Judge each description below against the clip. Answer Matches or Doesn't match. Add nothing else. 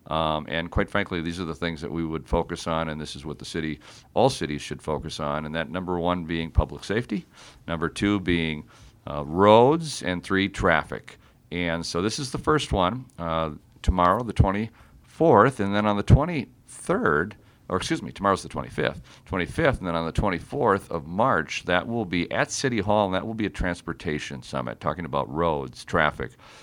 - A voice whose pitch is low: Matches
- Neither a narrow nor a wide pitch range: Matches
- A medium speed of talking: Matches